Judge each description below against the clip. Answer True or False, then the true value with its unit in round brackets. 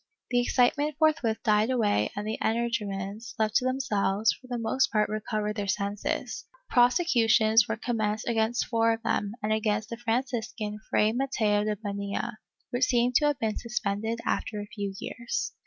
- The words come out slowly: False (165 wpm)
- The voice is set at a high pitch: True (220 Hz)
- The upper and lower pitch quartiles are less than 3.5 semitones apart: True (2.5 semitones)